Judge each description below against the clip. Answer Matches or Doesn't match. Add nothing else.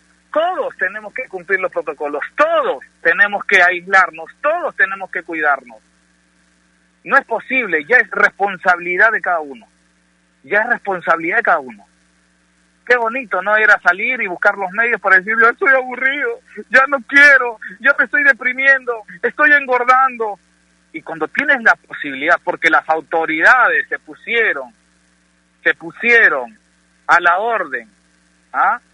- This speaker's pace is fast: Doesn't match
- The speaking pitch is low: Doesn't match